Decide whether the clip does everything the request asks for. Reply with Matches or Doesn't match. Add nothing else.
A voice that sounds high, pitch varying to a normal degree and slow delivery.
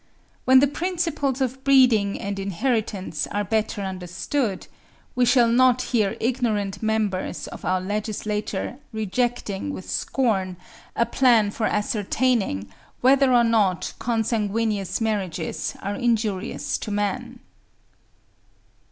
Matches